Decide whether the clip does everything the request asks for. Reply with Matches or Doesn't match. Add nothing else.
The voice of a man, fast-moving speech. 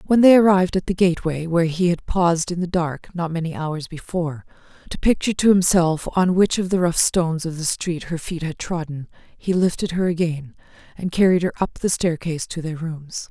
Doesn't match